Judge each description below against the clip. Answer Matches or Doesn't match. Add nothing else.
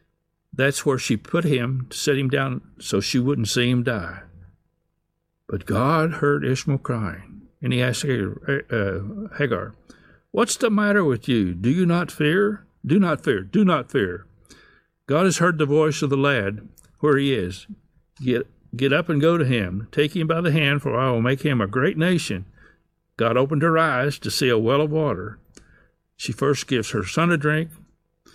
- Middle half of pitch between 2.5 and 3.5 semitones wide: Doesn't match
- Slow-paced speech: Doesn't match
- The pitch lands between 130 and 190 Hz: Matches